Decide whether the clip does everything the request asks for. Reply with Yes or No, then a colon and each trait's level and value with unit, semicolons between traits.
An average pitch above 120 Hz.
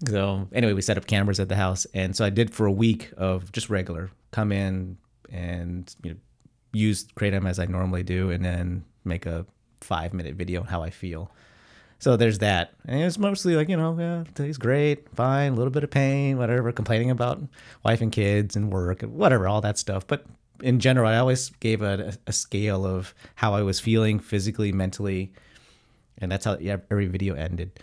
No: low, 105 Hz